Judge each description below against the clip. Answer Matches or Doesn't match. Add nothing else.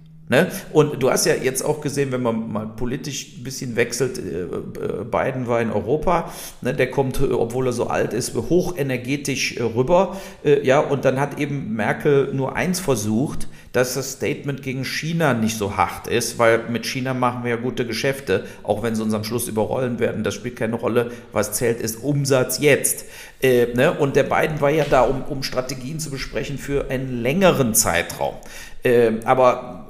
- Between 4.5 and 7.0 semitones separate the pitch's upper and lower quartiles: Doesn't match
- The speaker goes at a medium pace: Matches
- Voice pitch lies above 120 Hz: Matches